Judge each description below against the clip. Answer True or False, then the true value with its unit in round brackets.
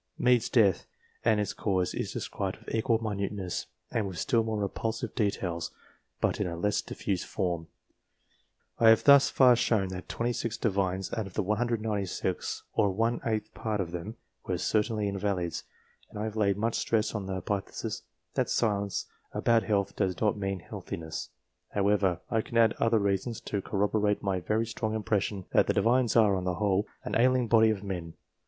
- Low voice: True (105 Hz)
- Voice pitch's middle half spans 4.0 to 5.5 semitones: False (2.6 semitones)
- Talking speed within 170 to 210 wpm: True (175 wpm)